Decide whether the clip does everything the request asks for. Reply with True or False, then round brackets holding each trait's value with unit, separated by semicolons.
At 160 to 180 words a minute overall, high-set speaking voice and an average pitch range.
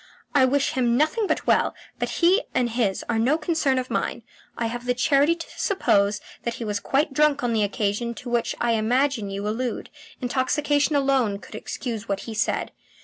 False (195 wpm; 245 Hz; 4.1 semitones)